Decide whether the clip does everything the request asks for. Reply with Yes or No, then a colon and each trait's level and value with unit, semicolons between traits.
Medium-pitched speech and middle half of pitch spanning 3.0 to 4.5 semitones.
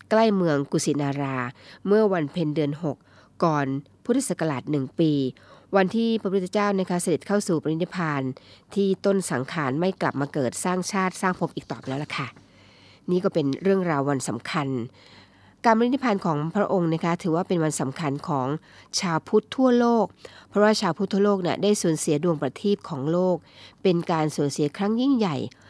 No: medium, 165 Hz; wide, 5.6 semitones